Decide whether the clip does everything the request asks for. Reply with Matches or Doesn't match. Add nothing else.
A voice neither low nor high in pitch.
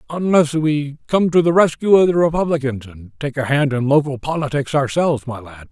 Matches